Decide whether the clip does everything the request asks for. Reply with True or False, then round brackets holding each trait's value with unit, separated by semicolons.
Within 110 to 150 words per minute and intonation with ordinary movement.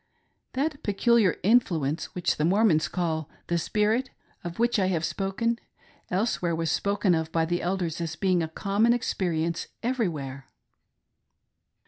True (145 wpm; 4.9 semitones)